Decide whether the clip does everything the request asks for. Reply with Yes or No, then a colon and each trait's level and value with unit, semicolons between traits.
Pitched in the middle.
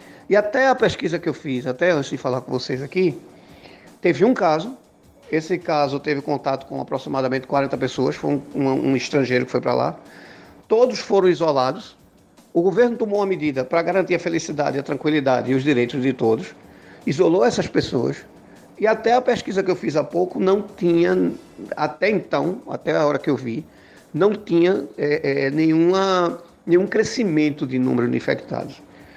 Yes: medium, 155 Hz